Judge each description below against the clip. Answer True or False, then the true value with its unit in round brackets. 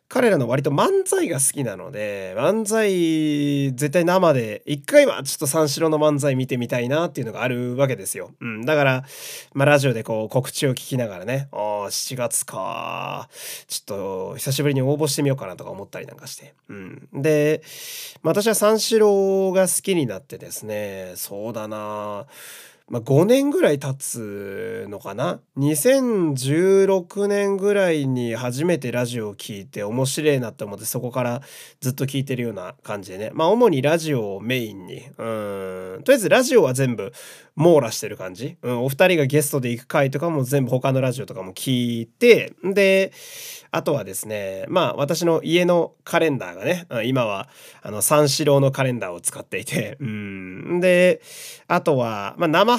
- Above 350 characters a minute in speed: False (330 characters per minute)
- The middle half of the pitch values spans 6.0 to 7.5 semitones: True (6.6 semitones)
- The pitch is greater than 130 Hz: True (140 Hz)